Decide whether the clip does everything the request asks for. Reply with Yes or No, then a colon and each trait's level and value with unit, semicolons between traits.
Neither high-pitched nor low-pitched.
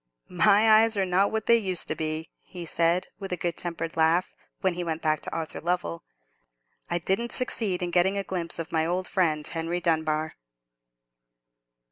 Yes: medium, 175 Hz